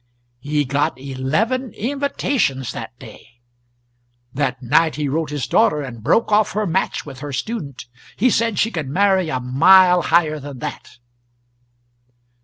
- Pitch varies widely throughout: Yes, wide, 6.7 semitones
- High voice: No, medium, 150 Hz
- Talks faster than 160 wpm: No, average, 145 wpm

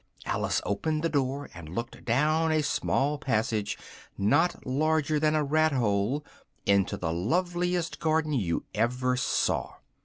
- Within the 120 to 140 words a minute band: Yes, slow, 135 wpm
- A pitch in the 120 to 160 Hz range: Yes, medium, 140 Hz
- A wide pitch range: Yes, wide, 6.1 semitones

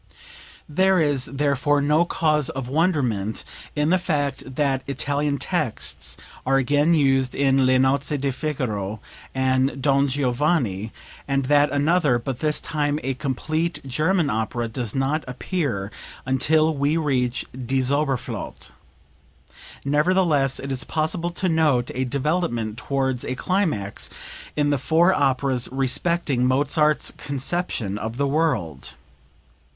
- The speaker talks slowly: Yes, slow, 125 wpm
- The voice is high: No, medium, 140 Hz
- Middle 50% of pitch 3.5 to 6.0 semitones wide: No, average, 3.0 semitones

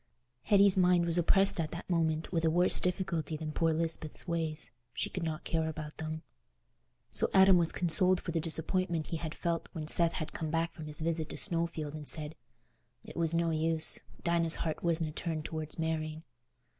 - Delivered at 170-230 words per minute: Yes, average, 185 wpm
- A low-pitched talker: No, medium, 165 Hz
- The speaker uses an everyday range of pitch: No, narrow, 1.4 semitones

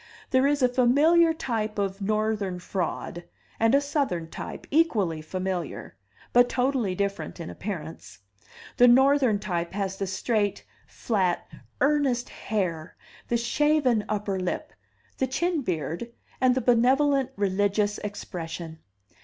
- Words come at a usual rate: No, slow, 125 wpm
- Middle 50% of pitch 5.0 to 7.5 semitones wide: Yes, wide, 5.6 semitones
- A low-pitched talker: No, high, 215 Hz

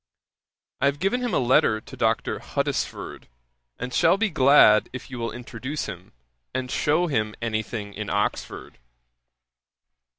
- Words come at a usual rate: Yes, average, 145 wpm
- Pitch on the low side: Yes, low, 125 Hz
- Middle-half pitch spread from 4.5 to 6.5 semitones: Yes, average, 5.2 semitones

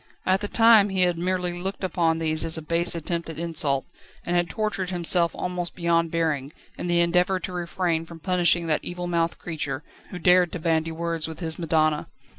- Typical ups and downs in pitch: No, narrow, 1.7 semitones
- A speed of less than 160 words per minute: No, average, 195 wpm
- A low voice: No, medium, 170 Hz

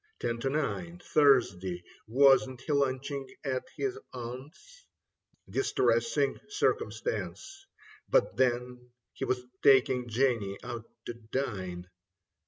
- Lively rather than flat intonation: No, average, 3.4 semitones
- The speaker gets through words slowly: Yes, slow, 100 wpm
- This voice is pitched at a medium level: No, low, 130 Hz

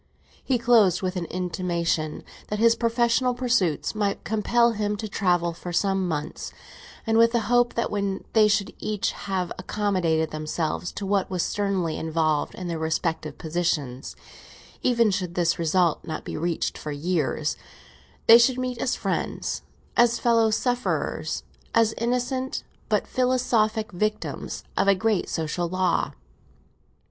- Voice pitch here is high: Yes, high, 195 Hz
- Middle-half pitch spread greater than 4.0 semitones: Yes, average, 5.2 semitones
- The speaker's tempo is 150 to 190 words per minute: No, average, 140 wpm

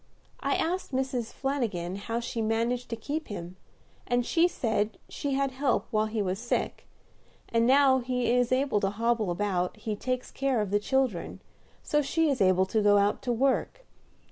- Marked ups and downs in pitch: No, average, 4.3 semitones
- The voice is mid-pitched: No, high, 235 Hz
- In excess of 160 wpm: Yes, average, 180 wpm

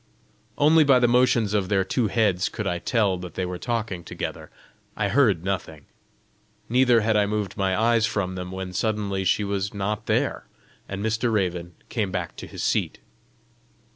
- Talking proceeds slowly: No, average, 175 wpm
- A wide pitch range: No, average, 3.4 semitones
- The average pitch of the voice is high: No, low, 100 Hz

